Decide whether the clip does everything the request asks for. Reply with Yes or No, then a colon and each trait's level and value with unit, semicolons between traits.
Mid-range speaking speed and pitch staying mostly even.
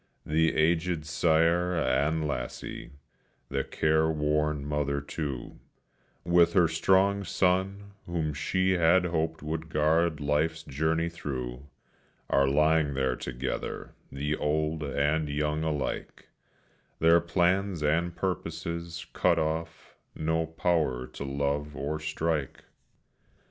No: slow, 110 wpm; narrow, 2.3 semitones